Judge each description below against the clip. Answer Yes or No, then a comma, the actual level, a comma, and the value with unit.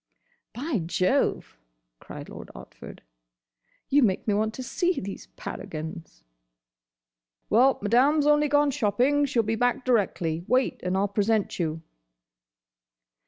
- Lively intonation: Yes, wide, 6.4 semitones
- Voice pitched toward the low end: No, high, 225 Hz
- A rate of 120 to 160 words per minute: Yes, slow, 135 wpm